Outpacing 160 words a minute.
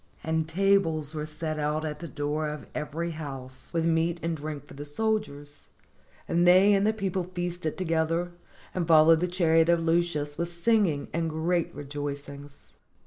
Yes: average, 170 wpm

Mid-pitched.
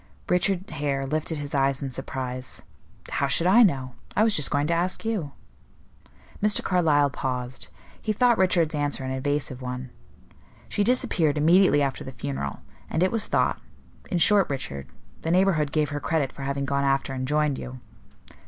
Yes: medium, 145 Hz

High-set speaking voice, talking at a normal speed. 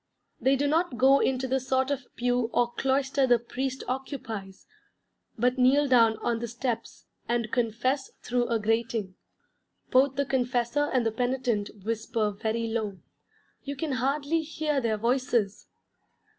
Yes: very high, 250 Hz; average, 145 wpm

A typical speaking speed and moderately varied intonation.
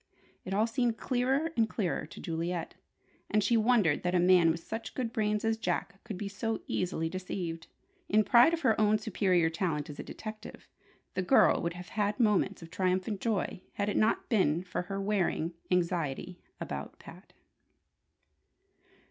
Yes: average, 170 wpm; average, 3.9 semitones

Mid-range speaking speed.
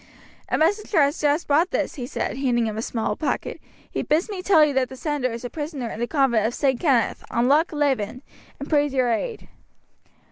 No: fast, 215 wpm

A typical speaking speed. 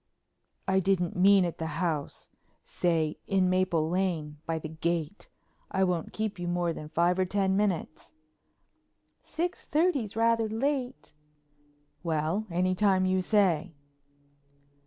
No: slow, 130 wpm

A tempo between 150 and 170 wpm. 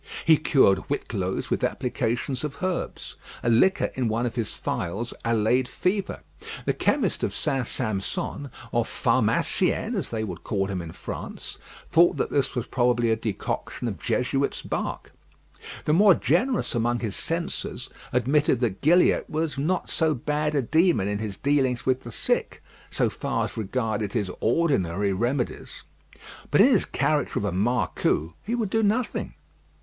Yes: average, 160 wpm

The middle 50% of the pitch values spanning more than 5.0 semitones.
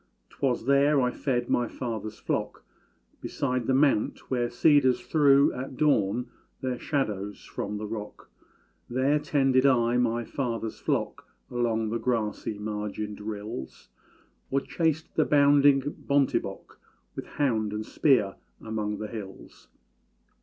No: average, 4.2 semitones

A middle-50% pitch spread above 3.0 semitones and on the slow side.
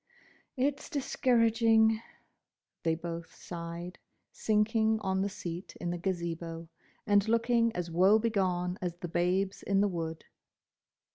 Yes: average, 4.4 semitones; slow, 125 wpm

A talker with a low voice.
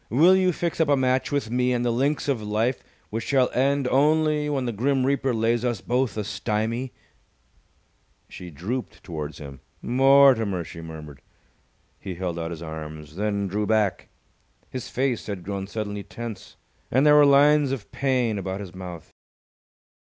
Yes: low, 115 Hz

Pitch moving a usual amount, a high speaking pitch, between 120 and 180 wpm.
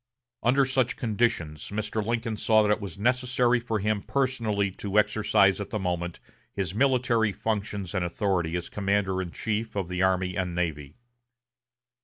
No: average, 3.5 semitones; low, 105 Hz; average, 160 wpm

